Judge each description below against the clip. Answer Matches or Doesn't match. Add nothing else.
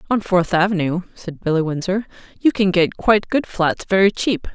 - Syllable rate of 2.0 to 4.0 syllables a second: Doesn't match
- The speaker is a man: Doesn't match